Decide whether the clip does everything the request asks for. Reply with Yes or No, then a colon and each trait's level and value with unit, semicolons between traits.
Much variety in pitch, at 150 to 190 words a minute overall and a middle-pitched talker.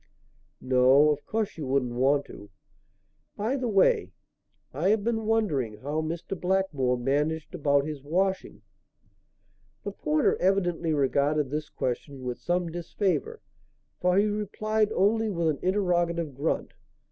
No: wide, 5.7 semitones; slow, 135 wpm; medium, 165 Hz